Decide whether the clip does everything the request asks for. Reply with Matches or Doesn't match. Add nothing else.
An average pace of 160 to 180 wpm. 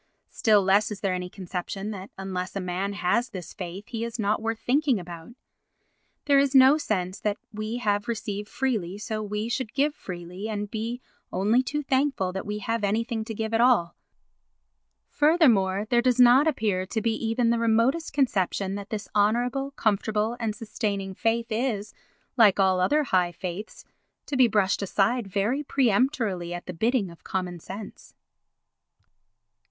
Matches